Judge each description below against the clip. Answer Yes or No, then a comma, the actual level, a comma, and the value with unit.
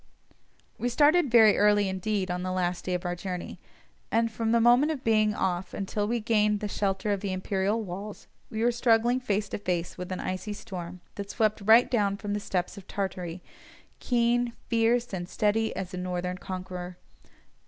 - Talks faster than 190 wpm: No, average, 185 wpm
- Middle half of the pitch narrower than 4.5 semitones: Yes, average, 3.6 semitones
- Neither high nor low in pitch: No, high, 205 Hz